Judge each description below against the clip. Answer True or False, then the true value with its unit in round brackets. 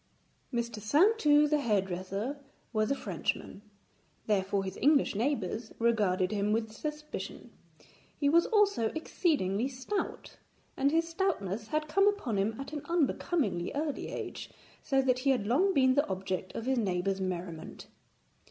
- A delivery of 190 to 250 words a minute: False (145 wpm)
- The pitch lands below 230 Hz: False (245 Hz)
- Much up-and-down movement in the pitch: True (7.1 semitones)